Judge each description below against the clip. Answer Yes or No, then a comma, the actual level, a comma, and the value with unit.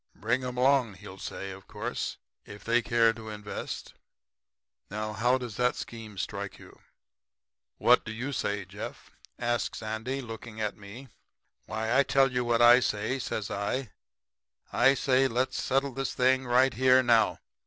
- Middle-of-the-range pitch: No, low, 120 Hz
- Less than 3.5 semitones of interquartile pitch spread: Yes, average, 3.1 semitones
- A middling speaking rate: Yes, average, 160 wpm